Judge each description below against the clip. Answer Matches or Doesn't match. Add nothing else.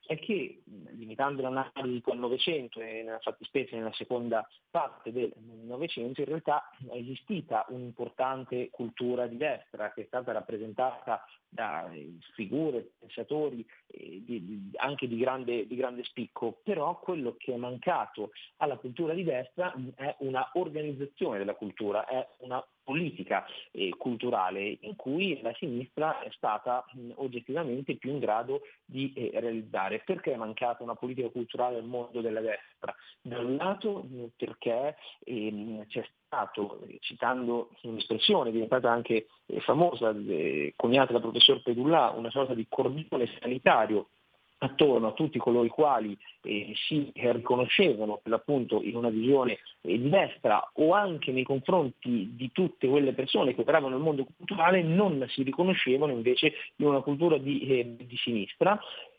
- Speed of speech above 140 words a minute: Matches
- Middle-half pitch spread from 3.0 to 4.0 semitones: Matches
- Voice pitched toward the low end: Matches